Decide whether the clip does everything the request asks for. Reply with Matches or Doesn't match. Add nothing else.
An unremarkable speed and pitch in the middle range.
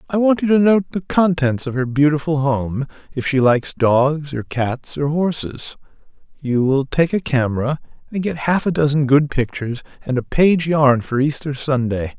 Matches